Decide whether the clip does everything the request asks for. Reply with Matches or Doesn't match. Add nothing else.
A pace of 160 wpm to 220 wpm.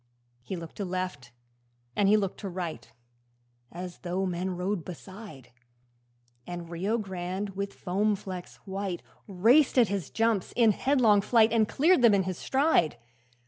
Doesn't match